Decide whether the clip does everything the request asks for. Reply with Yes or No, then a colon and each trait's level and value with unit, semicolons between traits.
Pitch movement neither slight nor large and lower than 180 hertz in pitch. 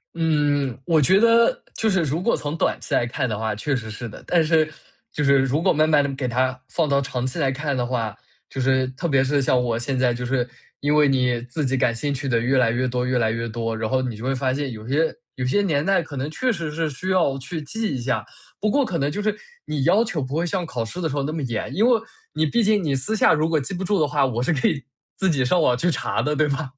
Yes: average, 4.3 semitones; medium, 140 Hz